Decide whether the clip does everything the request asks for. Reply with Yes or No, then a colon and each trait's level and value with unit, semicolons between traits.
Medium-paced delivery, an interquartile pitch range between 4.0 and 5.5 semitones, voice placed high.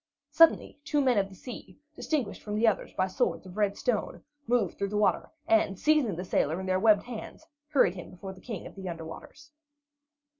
No: fast, 210 wpm; average, 4.8 semitones; high, 205 Hz